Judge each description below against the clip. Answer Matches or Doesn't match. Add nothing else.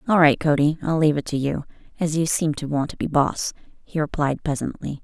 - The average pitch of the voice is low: Doesn't match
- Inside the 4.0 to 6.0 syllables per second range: Matches